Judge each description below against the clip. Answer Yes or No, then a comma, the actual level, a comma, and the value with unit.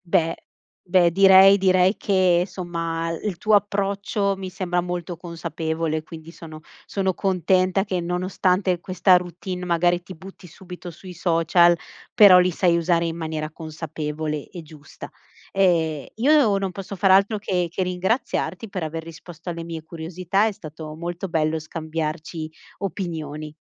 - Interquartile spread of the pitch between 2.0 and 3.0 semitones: Yes, narrow, 2.6 semitones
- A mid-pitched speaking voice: Yes, medium, 175 Hz